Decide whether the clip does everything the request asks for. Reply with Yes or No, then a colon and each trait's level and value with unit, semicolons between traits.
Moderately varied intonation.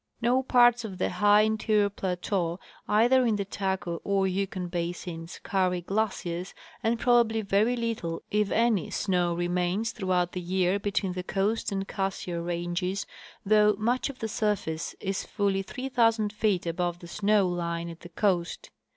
Yes: average, 3.5 semitones